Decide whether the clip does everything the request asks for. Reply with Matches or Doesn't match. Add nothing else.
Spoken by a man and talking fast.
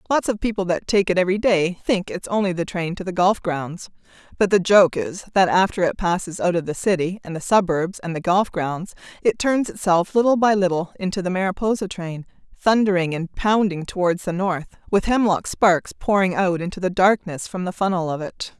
Doesn't match